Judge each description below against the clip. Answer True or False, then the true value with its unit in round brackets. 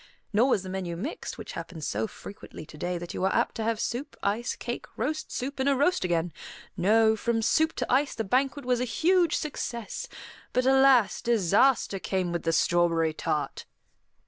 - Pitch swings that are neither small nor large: False (7.0 semitones)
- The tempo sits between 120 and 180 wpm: False (190 wpm)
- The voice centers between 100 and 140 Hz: False (225 Hz)